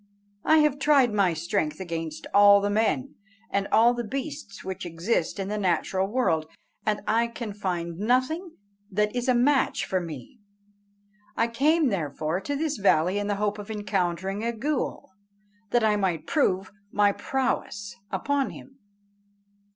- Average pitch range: Yes, average, 5.0 semitones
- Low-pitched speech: No, high, 205 Hz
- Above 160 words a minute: No, average, 155 wpm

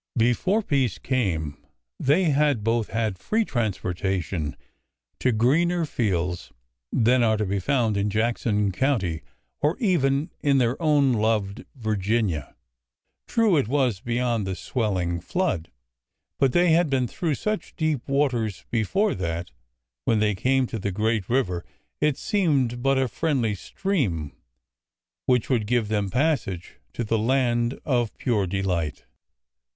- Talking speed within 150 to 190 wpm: No, average, 140 wpm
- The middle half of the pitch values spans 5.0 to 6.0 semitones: Yes, wide, 5.6 semitones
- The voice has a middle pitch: No, low, 120 Hz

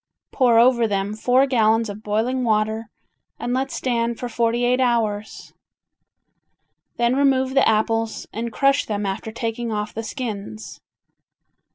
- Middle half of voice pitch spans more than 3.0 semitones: No, narrow, 2.4 semitones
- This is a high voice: Yes, high, 230 Hz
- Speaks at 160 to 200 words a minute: No, average, 140 wpm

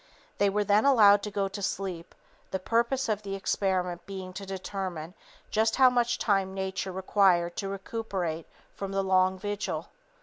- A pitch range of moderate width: No, narrow, 1.8 semitones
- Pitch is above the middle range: Yes, high, 195 Hz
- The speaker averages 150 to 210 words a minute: Yes, average, 165 wpm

